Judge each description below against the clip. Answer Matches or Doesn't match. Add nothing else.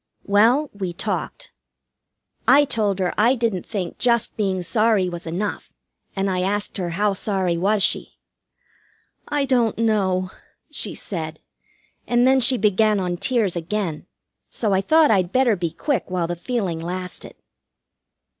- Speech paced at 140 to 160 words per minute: Matches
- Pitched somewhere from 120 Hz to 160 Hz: Doesn't match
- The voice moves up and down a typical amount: Matches